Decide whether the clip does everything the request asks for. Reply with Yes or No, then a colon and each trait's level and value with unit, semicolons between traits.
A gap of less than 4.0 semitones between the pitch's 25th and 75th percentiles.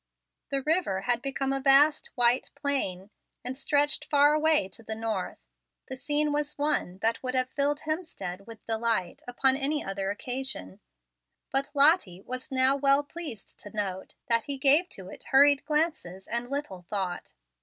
No: average, 5.1 semitones